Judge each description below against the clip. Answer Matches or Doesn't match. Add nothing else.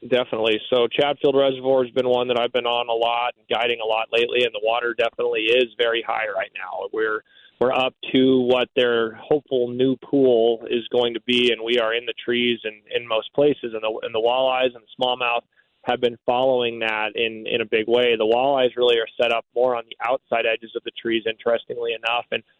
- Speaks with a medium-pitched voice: Doesn't match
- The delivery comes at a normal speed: Doesn't match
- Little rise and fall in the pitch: Matches